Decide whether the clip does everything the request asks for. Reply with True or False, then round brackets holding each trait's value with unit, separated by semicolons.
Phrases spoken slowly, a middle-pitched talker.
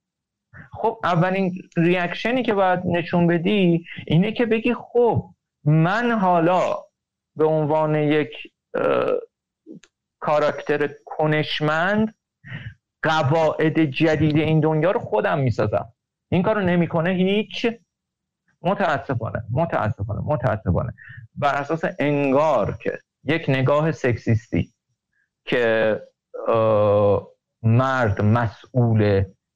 True (85 wpm; 155 Hz)